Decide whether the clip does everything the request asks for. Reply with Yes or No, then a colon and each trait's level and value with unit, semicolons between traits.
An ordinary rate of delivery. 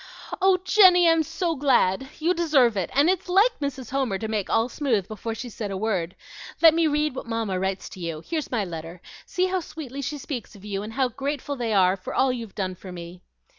No: fast, 225 wpm